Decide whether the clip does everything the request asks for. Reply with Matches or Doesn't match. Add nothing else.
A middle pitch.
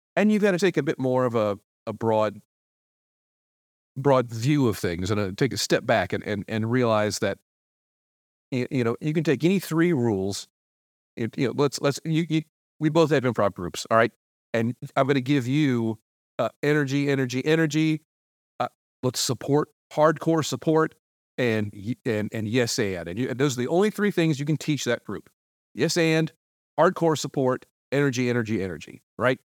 Doesn't match